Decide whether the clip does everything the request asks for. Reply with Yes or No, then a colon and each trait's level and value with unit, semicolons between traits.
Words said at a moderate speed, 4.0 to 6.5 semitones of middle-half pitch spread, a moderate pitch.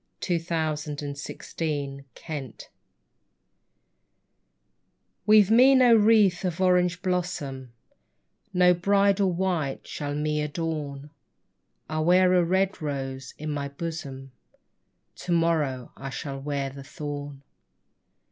No: slow, 110 wpm; average, 4.3 semitones; medium, 155 Hz